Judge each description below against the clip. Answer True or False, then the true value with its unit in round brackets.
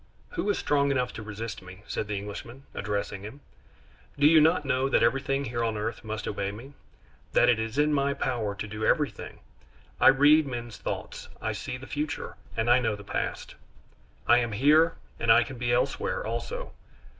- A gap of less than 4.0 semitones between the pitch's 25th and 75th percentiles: False (4.9 semitones)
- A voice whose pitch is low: True (125 Hz)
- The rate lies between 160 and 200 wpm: True (190 wpm)